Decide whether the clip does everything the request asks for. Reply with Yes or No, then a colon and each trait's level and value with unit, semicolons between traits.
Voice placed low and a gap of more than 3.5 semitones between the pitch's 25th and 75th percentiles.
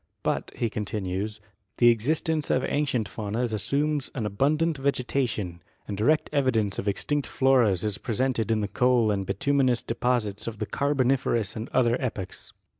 Yes: low, 120 Hz; average, 4.4 semitones